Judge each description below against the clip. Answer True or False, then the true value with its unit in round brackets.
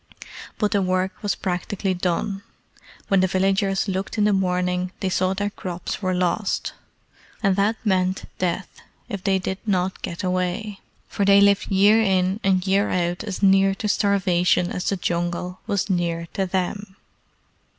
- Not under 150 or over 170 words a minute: True (160 wpm)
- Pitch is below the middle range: False (190 Hz)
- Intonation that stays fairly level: True (1.7 semitones)